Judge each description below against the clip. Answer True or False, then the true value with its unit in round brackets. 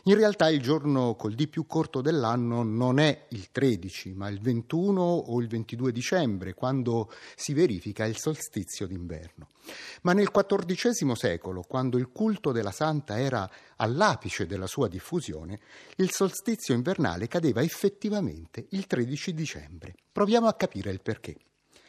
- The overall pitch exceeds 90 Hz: True (130 Hz)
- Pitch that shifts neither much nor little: False (8.2 semitones)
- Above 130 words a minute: True (145 wpm)